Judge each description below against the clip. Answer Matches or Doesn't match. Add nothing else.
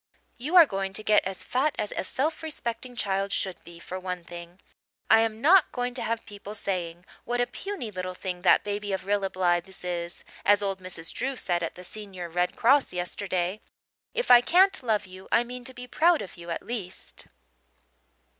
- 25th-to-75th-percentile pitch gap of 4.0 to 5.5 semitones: Matches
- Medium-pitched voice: Doesn't match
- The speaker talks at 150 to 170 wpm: Doesn't match